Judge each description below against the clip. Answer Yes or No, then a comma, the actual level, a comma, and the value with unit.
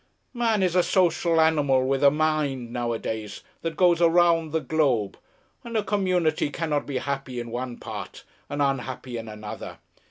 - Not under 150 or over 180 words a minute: Yes, average, 160 wpm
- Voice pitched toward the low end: No, medium, 145 Hz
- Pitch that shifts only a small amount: No, average, 5.2 semitones